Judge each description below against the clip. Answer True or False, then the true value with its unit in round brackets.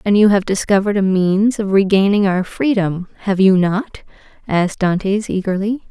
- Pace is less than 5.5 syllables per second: True (5.0 syllables/s)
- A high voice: True (195 Hz)